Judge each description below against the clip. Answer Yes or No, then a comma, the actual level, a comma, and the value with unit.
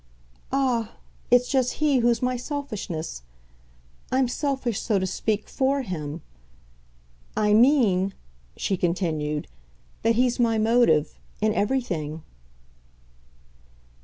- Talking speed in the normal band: No, slow, 105 wpm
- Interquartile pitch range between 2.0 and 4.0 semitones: No, wide, 5.5 semitones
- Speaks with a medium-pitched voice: No, high, 230 Hz